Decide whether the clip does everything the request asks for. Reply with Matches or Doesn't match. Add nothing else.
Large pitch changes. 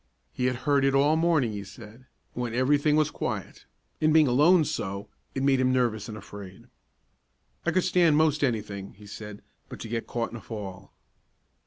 Matches